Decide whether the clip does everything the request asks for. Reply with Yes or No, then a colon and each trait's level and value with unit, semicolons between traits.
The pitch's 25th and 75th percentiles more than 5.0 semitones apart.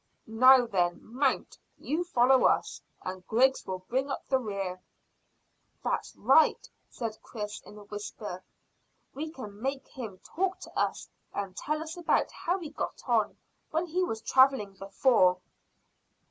Yes: wide, 5.5 semitones